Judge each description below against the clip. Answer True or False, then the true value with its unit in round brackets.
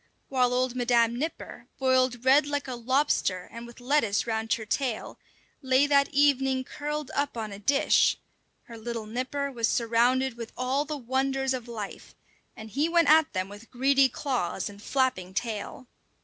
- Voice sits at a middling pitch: False (255 Hz)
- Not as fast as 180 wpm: True (165 wpm)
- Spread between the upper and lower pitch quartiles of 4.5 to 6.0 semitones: False (3.1 semitones)